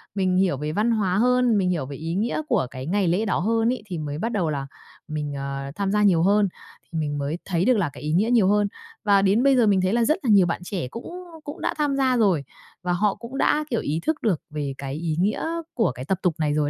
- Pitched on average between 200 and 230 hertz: No, high, 190 Hz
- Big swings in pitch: Yes, wide, 6.3 semitones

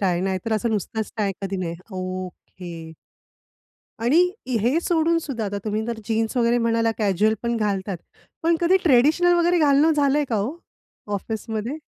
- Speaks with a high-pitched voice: Yes, high, 225 Hz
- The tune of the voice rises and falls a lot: Yes, wide, 6.6 semitones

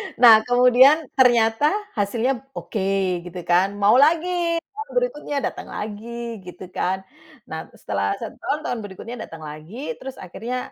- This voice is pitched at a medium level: No, high, 235 Hz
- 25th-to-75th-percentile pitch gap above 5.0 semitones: Yes, wide, 5.4 semitones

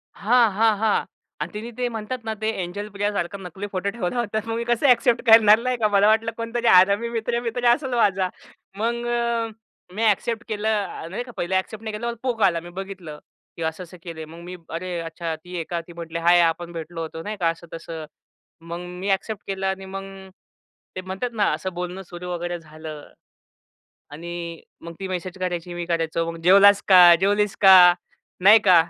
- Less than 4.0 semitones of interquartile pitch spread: No, average, 4.3 semitones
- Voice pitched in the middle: No, high, 195 Hz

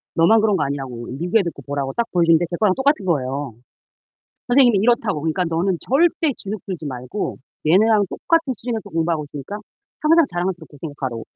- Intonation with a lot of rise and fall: Yes, wide, 7.0 semitones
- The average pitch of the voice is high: No, medium, 175 Hz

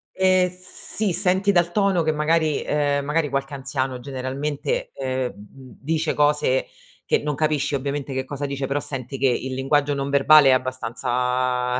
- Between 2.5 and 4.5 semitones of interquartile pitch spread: Yes, average, 2.9 semitones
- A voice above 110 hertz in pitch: Yes, medium, 140 Hz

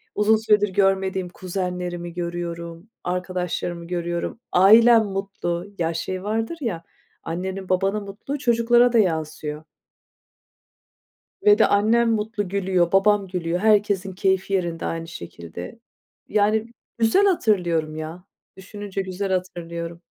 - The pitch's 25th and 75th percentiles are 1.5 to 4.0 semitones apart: Yes, average, 3.3 semitones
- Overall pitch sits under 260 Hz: Yes, high, 190 Hz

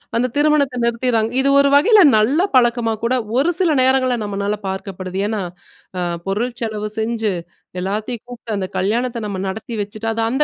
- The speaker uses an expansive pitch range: No, average, 3.6 semitones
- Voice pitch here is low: No, high, 230 Hz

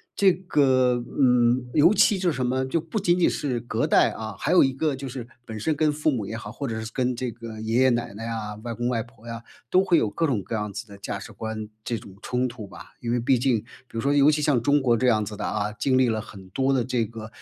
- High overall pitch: No, low, 120 Hz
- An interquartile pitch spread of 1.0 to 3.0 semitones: No, average, 3.6 semitones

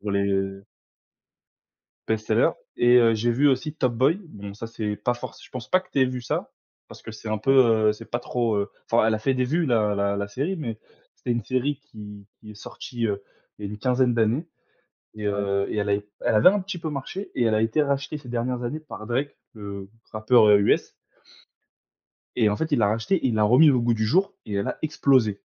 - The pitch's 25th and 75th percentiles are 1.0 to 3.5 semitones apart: No, average, 4.0 semitones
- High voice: No, low, 115 Hz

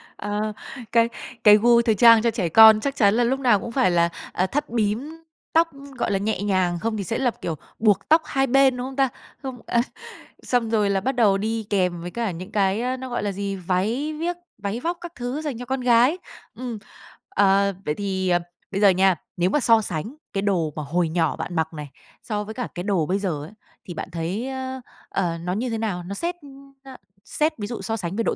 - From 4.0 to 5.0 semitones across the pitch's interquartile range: Yes, average, 4.7 semitones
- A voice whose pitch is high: Yes, high, 215 Hz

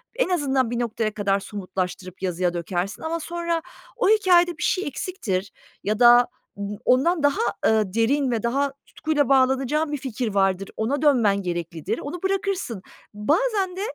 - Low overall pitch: No, high, 245 Hz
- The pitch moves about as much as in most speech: No, wide, 8.0 semitones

